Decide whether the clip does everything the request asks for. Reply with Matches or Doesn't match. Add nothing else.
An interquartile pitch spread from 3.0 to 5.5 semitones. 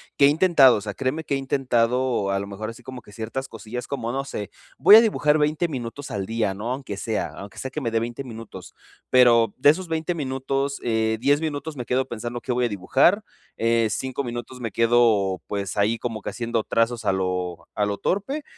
Matches